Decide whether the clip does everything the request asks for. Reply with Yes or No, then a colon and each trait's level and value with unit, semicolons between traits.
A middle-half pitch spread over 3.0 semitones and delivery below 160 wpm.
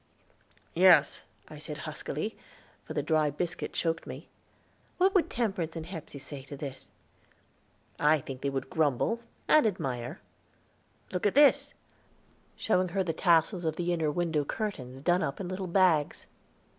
Yes: average, 4.3 semitones; average, 150 wpm